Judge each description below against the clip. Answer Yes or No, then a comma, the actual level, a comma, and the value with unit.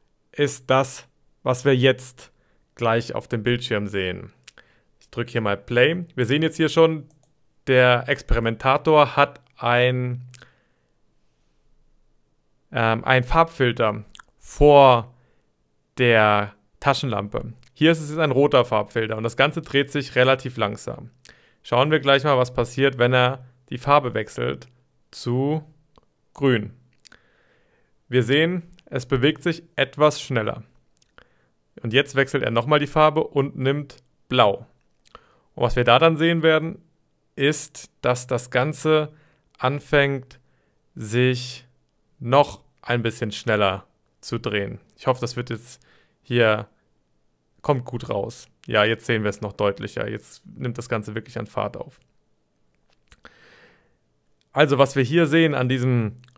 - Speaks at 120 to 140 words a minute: Yes, average, 130 wpm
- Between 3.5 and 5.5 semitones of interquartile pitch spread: Yes, average, 3.9 semitones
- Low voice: Yes, low, 125 Hz